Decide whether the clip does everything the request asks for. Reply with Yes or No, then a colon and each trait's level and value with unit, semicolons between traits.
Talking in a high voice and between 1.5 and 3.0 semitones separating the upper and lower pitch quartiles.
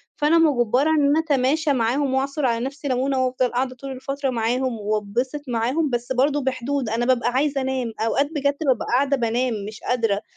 Yes: very high, 260 Hz; average, 2.7 semitones